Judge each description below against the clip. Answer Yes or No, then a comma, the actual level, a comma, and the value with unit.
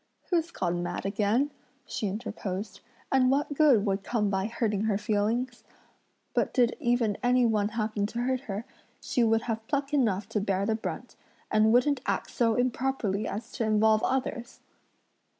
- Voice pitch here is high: Yes, high, 225 Hz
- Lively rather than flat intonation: No, average, 3.4 semitones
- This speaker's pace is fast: No, average, 165 wpm